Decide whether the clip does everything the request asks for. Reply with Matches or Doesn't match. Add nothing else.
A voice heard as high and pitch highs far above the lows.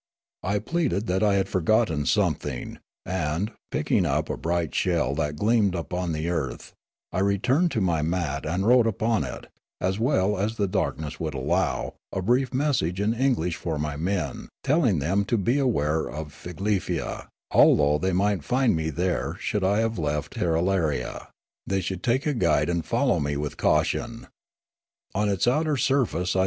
Doesn't match